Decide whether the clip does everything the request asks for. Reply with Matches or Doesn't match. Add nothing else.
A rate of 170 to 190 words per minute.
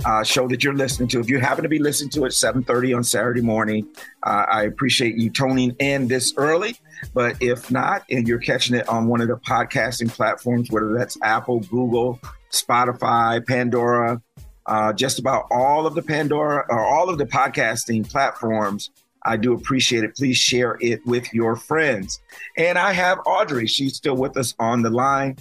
Matches